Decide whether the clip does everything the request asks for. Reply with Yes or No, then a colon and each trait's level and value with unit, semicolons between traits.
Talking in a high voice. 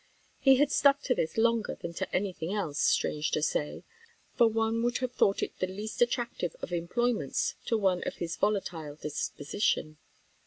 Yes: high, 205 Hz